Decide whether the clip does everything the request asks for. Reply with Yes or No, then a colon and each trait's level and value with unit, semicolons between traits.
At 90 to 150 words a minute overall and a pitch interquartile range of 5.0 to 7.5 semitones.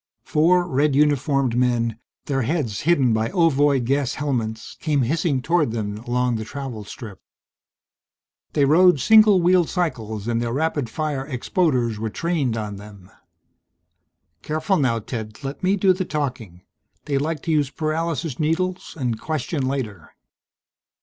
Yes: average, 145 wpm; wide, 5.4 semitones